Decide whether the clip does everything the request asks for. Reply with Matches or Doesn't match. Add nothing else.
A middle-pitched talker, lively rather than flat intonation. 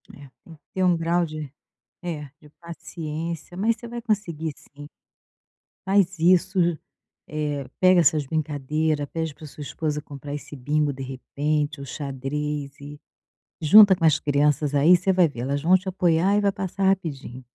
Doesn't match